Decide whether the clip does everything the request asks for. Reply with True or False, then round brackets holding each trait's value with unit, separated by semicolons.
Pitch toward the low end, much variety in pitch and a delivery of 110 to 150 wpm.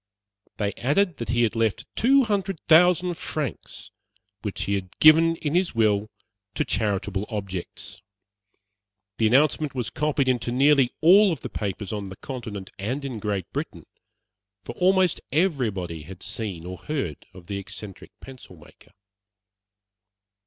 True (120 Hz; 7.6 semitones; 140 wpm)